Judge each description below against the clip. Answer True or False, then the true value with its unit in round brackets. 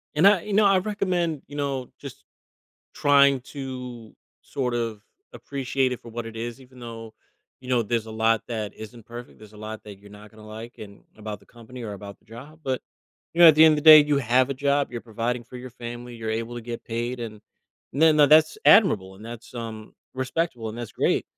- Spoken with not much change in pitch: False (3.8 semitones)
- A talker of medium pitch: False (120 Hz)